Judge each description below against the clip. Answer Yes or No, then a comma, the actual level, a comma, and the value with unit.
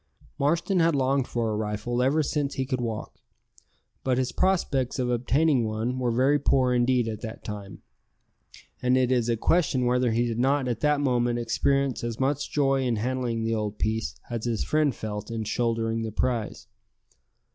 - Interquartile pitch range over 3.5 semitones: No, average, 3.0 semitones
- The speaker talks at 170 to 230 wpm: Yes, average, 180 wpm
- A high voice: No, low, 125 Hz